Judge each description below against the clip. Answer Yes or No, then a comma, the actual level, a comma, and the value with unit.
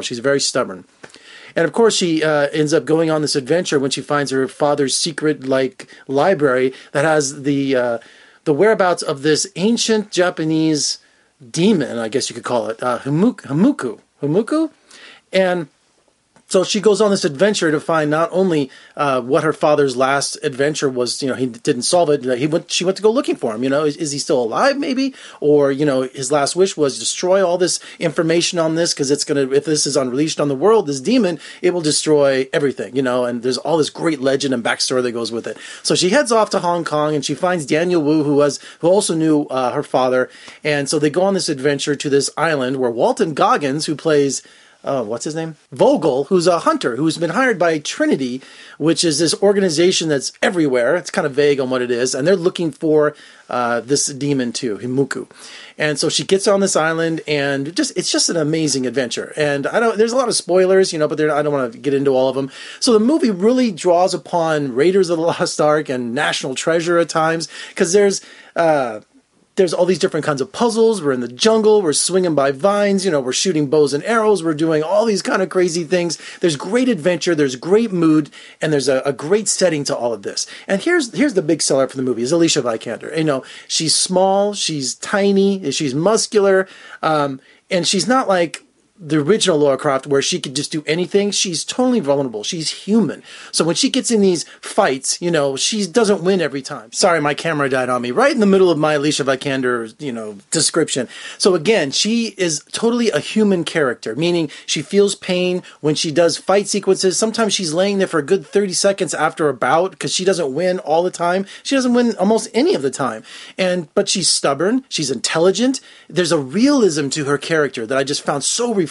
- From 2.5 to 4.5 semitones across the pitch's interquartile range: No, average, 5.1 semitones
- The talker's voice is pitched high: No, medium, 160 Hz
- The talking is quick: Yes, fast, 220 wpm